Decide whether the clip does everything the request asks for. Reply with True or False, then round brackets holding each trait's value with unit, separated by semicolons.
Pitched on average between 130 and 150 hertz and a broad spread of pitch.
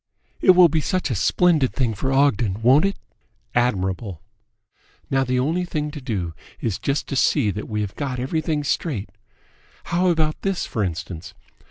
True (135 Hz; 6.5 semitones)